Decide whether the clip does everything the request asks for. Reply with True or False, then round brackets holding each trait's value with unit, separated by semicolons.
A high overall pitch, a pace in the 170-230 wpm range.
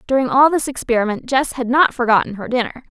True (250 Hz; 200 wpm)